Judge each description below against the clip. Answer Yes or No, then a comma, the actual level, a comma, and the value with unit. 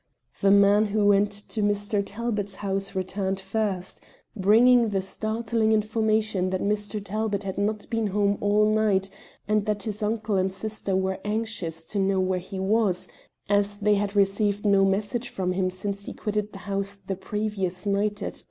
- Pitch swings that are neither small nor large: No, narrow, 1.6 semitones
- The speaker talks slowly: No, average, 175 wpm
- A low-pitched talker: No, high, 205 Hz